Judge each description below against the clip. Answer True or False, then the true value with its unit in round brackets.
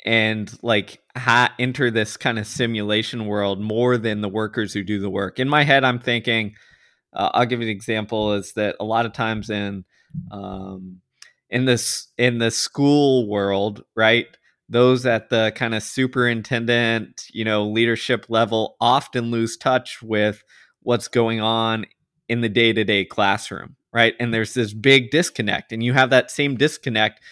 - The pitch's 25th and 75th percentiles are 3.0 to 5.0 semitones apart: False (2.4 semitones)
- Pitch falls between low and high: False (115 Hz)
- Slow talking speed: False (165 wpm)